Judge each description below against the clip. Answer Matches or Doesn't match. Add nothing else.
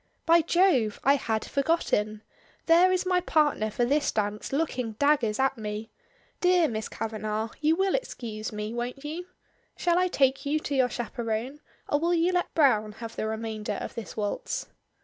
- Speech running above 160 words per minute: Matches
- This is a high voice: Matches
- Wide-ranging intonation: Matches